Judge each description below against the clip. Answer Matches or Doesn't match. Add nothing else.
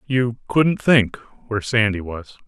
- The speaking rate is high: Doesn't match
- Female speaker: Doesn't match